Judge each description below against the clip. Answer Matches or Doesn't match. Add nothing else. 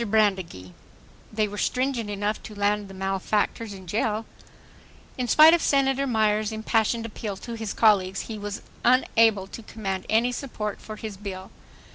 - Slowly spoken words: Doesn't match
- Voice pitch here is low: Doesn't match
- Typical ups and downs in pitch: Doesn't match